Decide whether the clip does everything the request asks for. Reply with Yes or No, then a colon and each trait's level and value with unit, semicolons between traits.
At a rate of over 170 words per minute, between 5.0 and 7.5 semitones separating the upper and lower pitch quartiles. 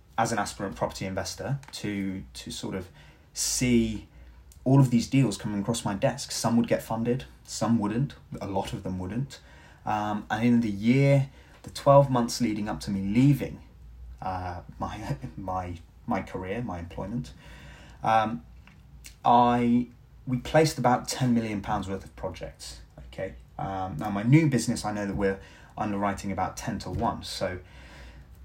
No: average, 160 wpm; average, 5.3 semitones